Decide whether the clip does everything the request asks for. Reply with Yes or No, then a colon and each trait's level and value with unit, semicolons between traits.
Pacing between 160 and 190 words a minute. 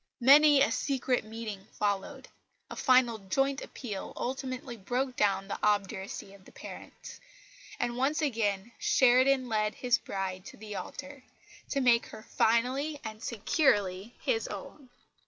No: slow, 135 wpm